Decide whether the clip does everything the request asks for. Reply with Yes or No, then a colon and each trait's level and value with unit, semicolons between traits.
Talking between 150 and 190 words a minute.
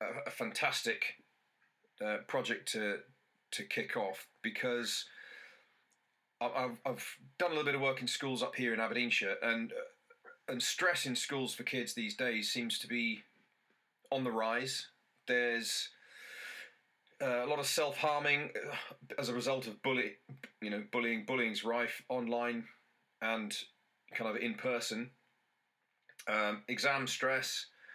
No: slow, 135 wpm